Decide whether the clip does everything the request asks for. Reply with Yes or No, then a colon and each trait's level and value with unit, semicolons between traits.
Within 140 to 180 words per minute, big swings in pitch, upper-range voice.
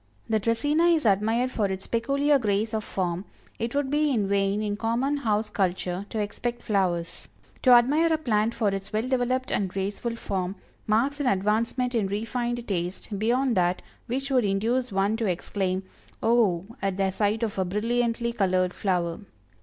No: average, 170 wpm; average, 3.8 semitones; high, 220 Hz